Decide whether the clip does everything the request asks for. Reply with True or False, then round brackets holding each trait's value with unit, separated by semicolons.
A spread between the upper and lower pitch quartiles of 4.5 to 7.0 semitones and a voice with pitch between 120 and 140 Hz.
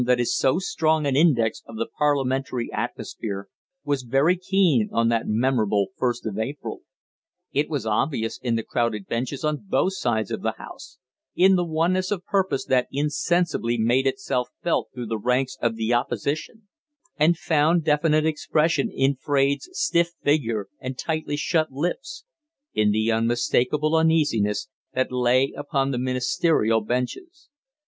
True (5.1 semitones; 135 Hz)